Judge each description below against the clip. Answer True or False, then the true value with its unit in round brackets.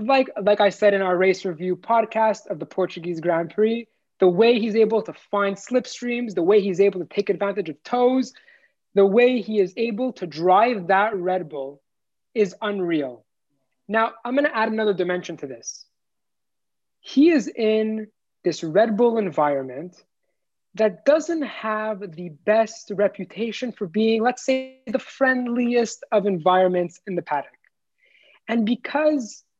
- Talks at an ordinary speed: True (155 wpm)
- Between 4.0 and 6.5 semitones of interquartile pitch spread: True (4.5 semitones)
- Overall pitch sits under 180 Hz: False (215 Hz)